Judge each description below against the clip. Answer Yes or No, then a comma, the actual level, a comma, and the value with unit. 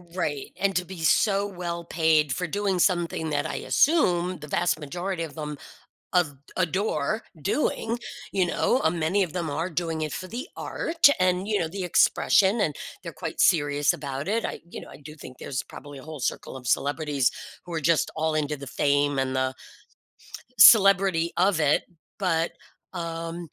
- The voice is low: No, medium, 165 Hz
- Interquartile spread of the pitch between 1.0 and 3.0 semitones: No, average, 3.9 semitones